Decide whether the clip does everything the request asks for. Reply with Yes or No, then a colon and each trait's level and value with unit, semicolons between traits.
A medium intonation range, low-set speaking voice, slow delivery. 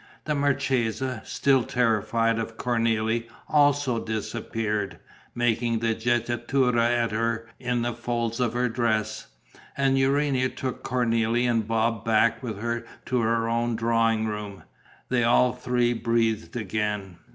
No: narrow, 1.7 semitones; low, 115 Hz; slow, 130 wpm